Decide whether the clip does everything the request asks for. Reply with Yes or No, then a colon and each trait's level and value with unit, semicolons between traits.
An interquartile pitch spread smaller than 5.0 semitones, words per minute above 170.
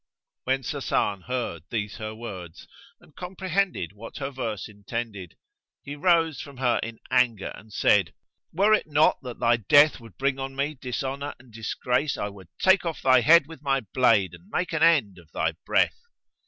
No: average, 5.3 semitones; average, 180 wpm